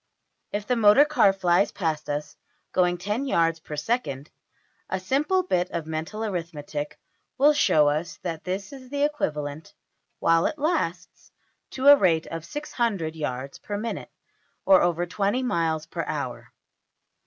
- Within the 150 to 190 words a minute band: No, slow, 135 wpm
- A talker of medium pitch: Yes, medium, 180 Hz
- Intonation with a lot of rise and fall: Yes, wide, 6.9 semitones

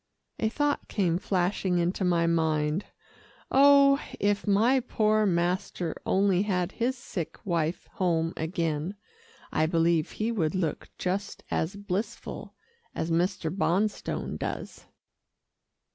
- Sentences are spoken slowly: Yes, slow, 115 wpm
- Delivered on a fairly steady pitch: No, average, 3.8 semitones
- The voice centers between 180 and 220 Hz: Yes, medium, 185 Hz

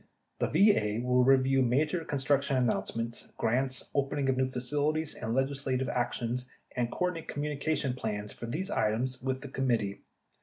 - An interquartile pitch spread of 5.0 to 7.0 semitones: No, average, 2.7 semitones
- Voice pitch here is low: Yes, low, 130 Hz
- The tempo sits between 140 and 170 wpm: Yes, average, 145 wpm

